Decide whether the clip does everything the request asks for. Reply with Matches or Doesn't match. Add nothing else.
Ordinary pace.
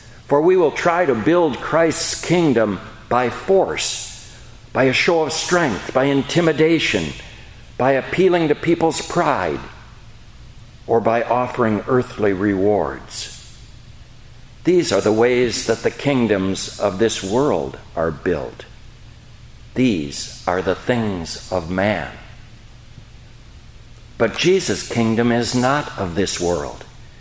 Doesn't match